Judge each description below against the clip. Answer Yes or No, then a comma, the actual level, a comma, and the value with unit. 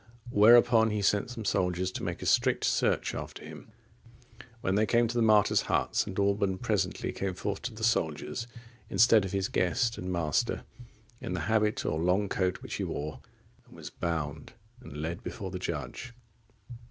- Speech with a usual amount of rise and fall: Yes, average, 4.0 semitones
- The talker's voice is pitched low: Yes, low, 100 Hz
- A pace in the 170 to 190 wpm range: Yes, average, 175 wpm